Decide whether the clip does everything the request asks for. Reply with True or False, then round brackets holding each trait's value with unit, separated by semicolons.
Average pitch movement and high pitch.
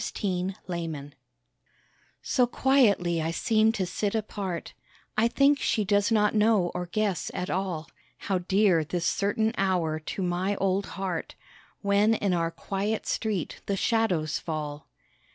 True (3.6 semitones; 195 Hz)